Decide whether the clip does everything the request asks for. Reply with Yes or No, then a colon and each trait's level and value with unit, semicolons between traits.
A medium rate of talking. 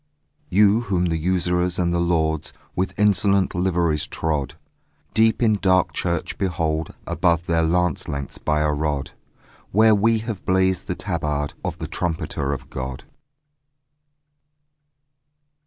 No: slow, 130 wpm